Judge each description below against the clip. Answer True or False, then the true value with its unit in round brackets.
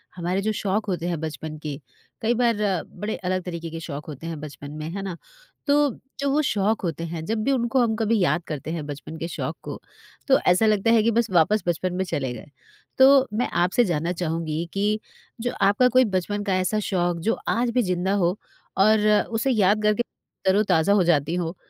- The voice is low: False (190 Hz)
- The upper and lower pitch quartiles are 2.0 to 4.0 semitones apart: False (4.7 semitones)